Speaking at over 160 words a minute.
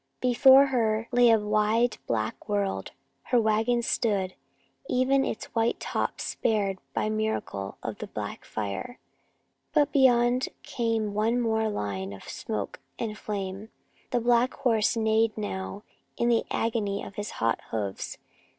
No: average, 140 wpm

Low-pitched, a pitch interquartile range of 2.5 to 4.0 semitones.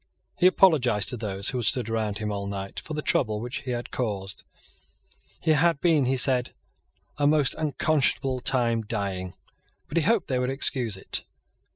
No: low, 125 Hz; wide, 5.5 semitones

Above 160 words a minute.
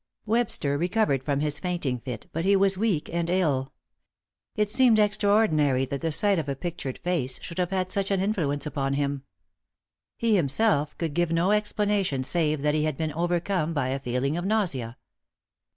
Yes: average, 180 wpm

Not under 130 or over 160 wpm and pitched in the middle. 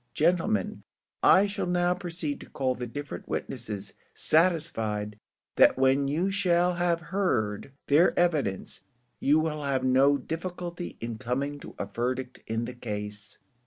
Yes: average, 140 wpm; medium, 145 Hz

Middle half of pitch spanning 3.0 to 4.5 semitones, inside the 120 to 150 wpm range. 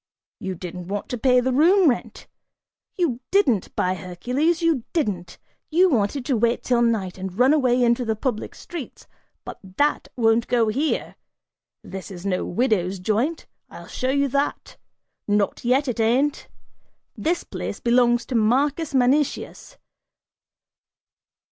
No: average, 5.3 semitones; average, 140 wpm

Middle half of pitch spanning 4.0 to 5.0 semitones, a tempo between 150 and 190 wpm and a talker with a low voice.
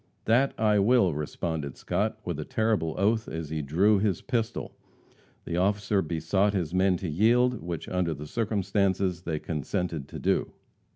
Yes: average, 4.6 semitones; average, 160 wpm; very low, 95 Hz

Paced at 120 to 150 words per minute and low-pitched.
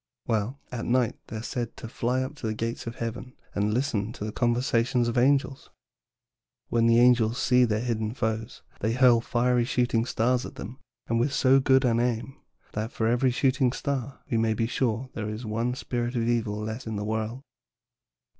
No: average, 200 wpm; low, 120 Hz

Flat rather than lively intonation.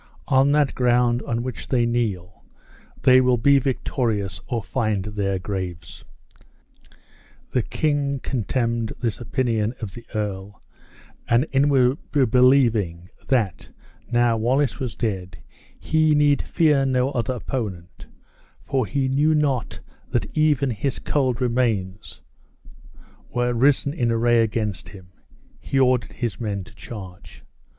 No: average, 4.0 semitones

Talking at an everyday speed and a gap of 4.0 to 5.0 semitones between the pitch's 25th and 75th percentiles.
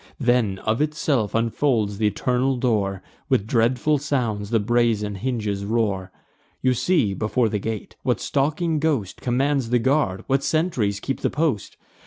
Yes: average, 150 wpm; average, 4.6 semitones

